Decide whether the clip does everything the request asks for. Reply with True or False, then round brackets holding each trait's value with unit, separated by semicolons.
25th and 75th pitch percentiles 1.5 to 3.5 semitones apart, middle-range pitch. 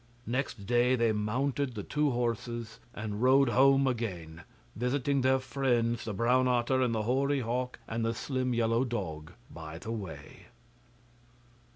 False (2.6 semitones; 120 Hz)